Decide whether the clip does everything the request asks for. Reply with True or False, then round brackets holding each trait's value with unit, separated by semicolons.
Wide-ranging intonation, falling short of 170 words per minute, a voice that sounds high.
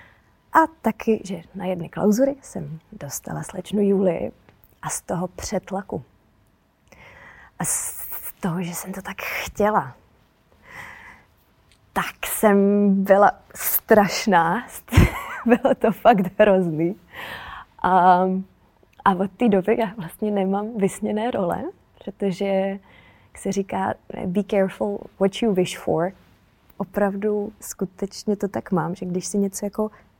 False (2.4 semitones; 120 wpm; 195 Hz)